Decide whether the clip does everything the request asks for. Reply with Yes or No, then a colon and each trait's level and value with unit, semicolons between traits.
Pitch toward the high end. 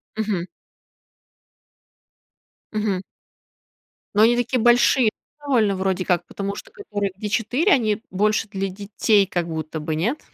Yes: high, 205 Hz